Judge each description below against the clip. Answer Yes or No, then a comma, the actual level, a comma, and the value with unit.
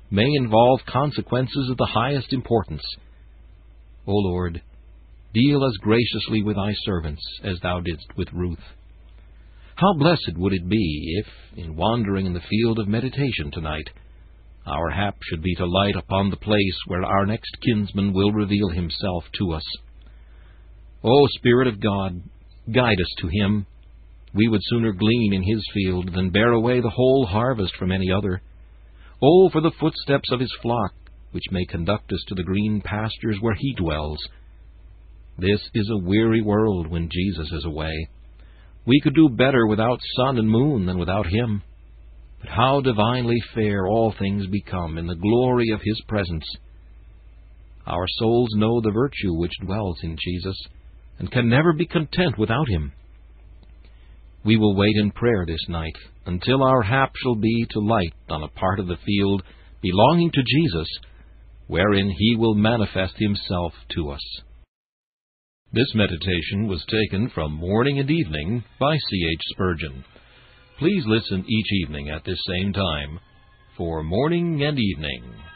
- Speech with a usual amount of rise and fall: Yes, average, 4.7 semitones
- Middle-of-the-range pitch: No, low, 100 Hz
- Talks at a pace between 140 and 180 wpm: Yes, average, 155 wpm